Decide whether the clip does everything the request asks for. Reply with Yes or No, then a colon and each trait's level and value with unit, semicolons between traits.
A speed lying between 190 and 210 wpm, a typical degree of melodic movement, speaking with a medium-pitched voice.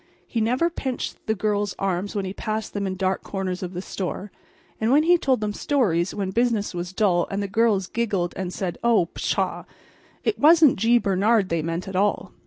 No: average, 200 wpm; average, 3.7 semitones; high, 205 Hz